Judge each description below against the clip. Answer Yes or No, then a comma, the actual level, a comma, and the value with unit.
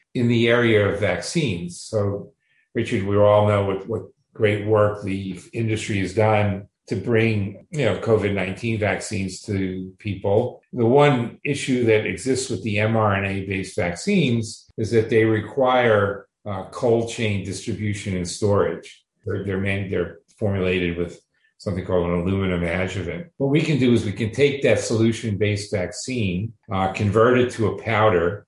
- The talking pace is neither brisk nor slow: Yes, average, 155 wpm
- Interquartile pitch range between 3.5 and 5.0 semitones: No, average, 3.0 semitones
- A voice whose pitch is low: Yes, low, 105 Hz